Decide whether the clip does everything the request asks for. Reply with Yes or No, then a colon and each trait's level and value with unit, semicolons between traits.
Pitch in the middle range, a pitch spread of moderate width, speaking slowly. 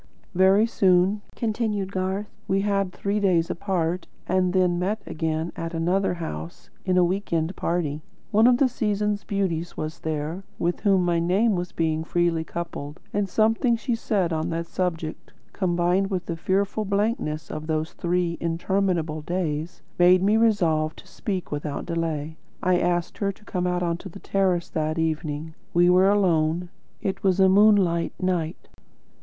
No: medium, 180 Hz; average, 3.1 semitones; average, 160 wpm